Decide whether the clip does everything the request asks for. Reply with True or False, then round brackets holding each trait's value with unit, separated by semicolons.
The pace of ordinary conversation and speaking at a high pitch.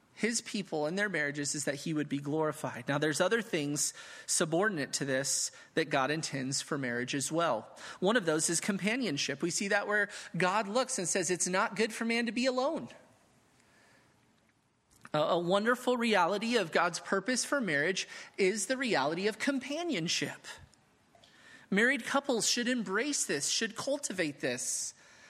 True (160 wpm; 195 Hz)